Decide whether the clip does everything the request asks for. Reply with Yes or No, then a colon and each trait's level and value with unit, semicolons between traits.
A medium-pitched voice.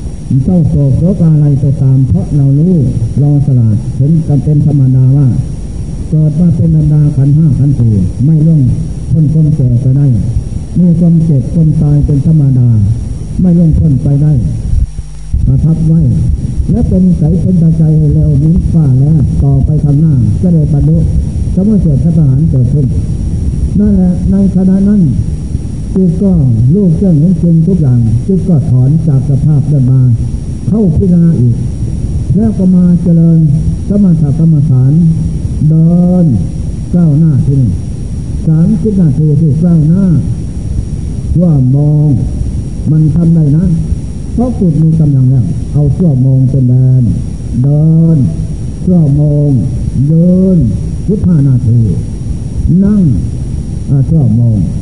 Yes: medium, 145 Hz